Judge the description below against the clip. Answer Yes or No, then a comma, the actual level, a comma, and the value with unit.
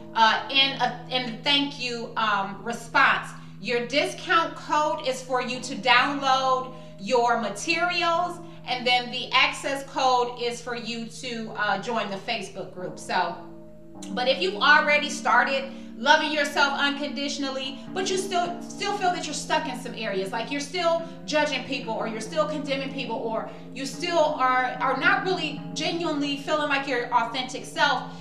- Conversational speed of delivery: Yes, average, 160 wpm